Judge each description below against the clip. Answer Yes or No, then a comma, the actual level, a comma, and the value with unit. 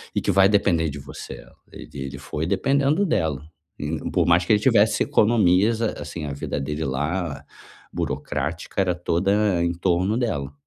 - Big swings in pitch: Yes, wide, 5.8 semitones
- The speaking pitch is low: Yes, very low, 90 Hz